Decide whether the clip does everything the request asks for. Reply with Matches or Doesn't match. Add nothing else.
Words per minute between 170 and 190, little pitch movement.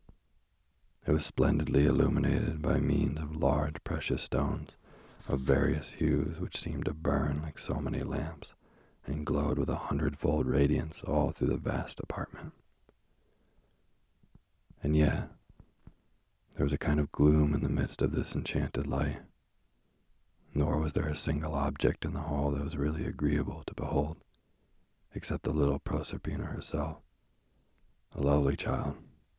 Doesn't match